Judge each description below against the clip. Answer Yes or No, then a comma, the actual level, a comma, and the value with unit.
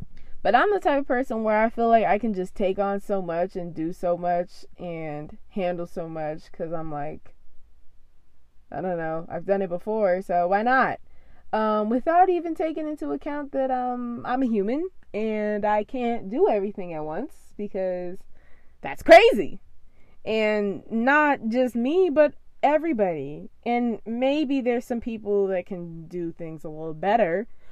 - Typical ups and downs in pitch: No, wide, 6.2 semitones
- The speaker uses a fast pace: No, average, 165 wpm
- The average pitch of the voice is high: Yes, high, 205 Hz